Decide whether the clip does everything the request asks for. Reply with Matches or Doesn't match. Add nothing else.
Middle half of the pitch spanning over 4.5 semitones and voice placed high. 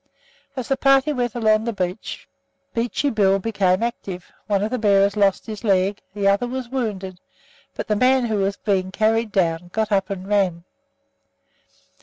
Doesn't match